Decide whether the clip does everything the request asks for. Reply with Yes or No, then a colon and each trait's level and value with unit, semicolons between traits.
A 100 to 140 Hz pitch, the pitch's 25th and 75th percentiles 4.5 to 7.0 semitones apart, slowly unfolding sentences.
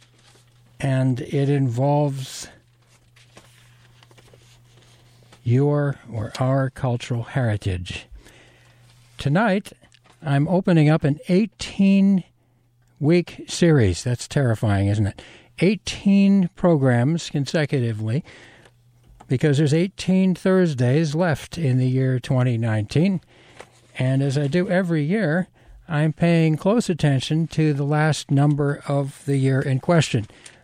Yes: low, 135 Hz; average, 4.8 semitones; slow, 100 wpm